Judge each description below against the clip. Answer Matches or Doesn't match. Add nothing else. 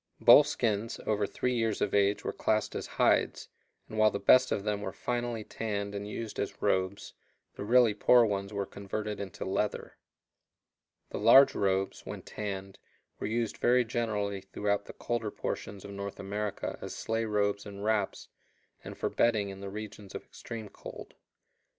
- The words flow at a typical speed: Matches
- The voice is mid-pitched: Doesn't match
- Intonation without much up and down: Matches